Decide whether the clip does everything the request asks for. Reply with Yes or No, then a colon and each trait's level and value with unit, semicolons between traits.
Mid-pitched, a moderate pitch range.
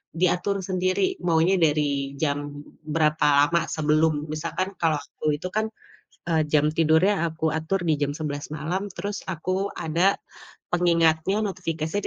Yes: medium, 160 Hz; average, 3.3 semitones